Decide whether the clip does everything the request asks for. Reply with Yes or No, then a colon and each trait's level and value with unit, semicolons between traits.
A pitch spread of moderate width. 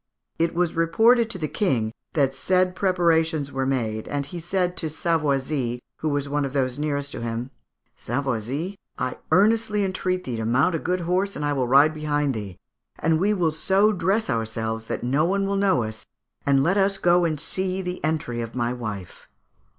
No: wide, 5.9 semitones